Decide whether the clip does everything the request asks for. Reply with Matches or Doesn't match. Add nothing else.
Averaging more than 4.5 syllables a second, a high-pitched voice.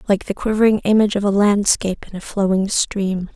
Matches